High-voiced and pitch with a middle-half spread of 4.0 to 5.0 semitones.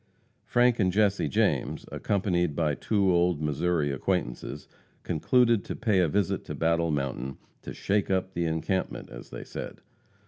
No: very low, 90 Hz; average, 4.5 semitones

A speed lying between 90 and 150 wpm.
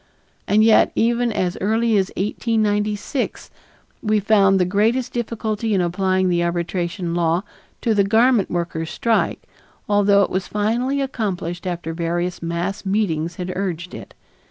Yes: average, 140 wpm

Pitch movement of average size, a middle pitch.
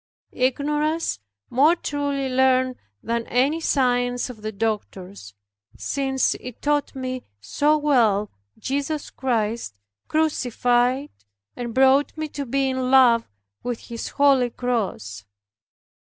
No: average, 3.2 semitones; very high, 255 Hz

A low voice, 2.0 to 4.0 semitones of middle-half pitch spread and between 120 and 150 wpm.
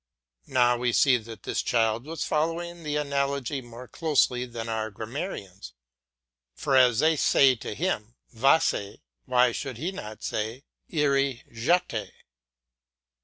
No: low, 125 Hz; average, 4.4 semitones; average, 145 wpm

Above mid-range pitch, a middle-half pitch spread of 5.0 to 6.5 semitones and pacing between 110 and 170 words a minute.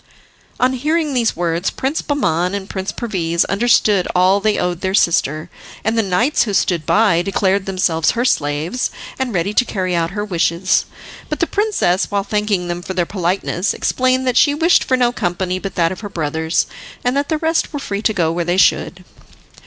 No: high, 195 Hz; wide, 5.6 semitones; average, 195 wpm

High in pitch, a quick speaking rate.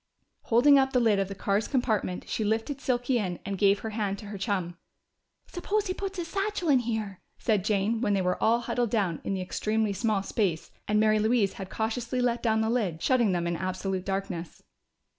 Yes: high, 215 Hz; fast, 210 wpm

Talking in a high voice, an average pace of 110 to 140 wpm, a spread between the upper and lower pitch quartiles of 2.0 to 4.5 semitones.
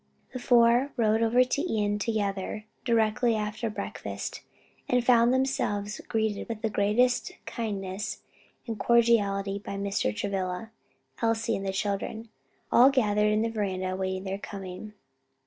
Yes: high, 215 Hz; slow, 135 wpm; average, 2.8 semitones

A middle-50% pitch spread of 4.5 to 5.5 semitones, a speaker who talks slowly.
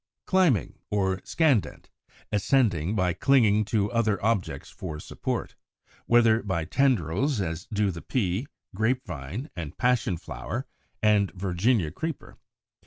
Yes: average, 5.0 semitones; slow, 125 wpm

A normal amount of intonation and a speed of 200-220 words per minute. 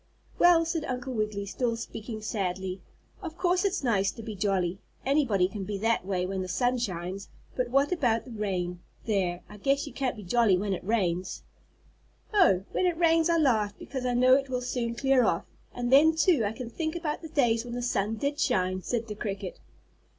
No: wide, 5.8 semitones; fast, 205 wpm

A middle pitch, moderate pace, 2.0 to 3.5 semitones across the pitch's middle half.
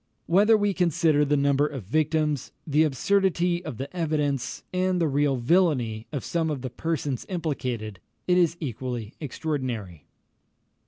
No: medium, 150 Hz; average, 145 wpm; average, 4.7 semitones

